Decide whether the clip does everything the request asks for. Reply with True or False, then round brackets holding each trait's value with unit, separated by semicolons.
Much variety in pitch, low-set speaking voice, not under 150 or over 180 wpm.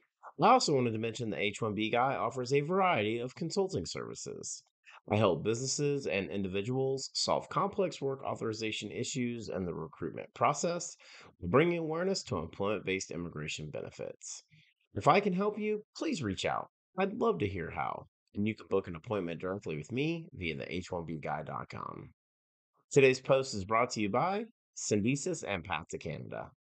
True (8.4 semitones; 120 Hz; 170 wpm)